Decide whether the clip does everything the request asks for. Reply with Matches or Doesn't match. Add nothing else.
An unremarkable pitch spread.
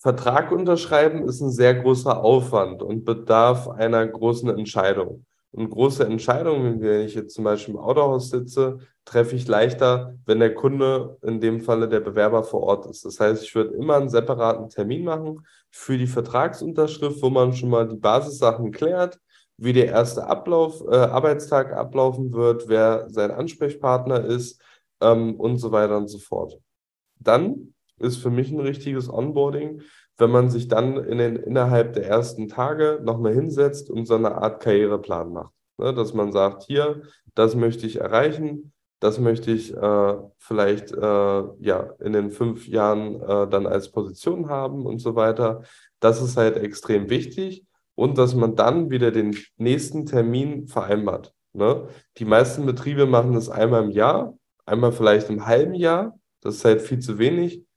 Matches